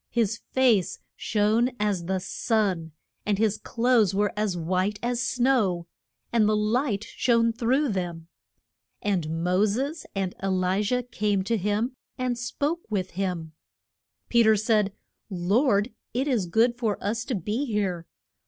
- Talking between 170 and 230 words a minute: No, average, 150 wpm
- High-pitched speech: Yes, high, 210 Hz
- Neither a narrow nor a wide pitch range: Yes, average, 3.9 semitones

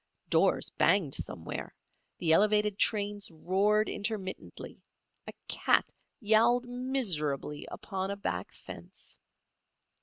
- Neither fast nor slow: No, slow, 95 wpm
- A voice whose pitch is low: No, high, 205 Hz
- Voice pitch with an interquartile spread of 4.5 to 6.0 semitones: No, average, 3.0 semitones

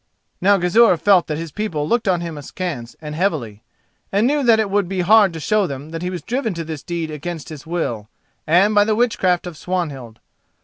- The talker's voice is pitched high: No, medium, 175 Hz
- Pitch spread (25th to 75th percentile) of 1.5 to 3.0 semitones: No, average, 4.8 semitones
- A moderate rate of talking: No, fast, 215 wpm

